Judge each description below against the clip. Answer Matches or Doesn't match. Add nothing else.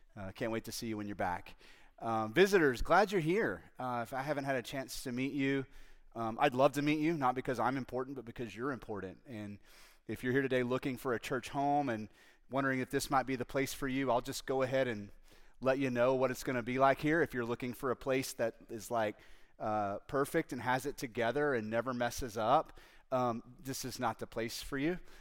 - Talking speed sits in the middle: Doesn't match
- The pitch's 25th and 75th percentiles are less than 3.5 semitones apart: Matches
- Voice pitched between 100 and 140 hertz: Matches